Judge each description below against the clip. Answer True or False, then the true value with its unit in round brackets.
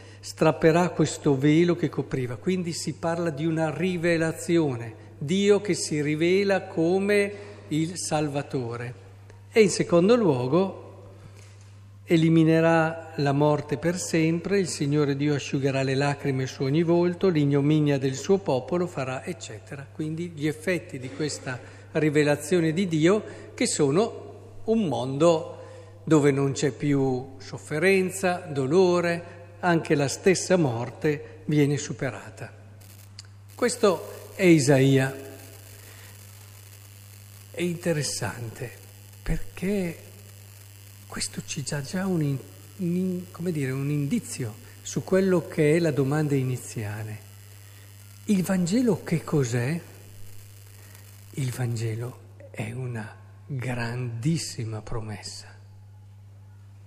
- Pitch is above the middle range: False (140 Hz)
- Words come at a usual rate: False (105 wpm)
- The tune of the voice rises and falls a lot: True (8.2 semitones)